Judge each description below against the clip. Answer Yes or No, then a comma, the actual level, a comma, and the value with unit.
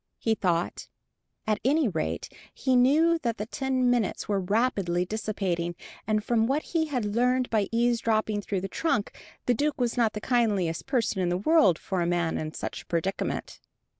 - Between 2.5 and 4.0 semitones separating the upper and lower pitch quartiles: No, average, 4.7 semitones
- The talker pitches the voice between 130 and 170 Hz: No, high, 220 Hz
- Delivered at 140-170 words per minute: No, average, 180 wpm